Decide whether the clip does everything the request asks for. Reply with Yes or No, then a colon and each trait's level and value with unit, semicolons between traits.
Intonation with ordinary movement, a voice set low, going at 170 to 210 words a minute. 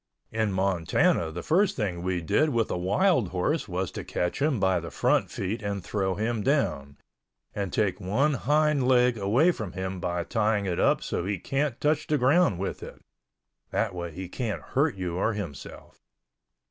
No: wide, 6.2 semitones; low, 100 Hz; average, 185 wpm